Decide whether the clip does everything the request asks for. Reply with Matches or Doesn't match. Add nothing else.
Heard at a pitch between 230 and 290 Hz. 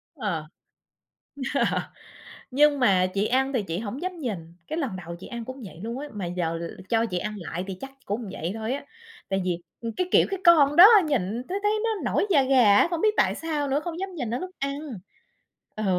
Matches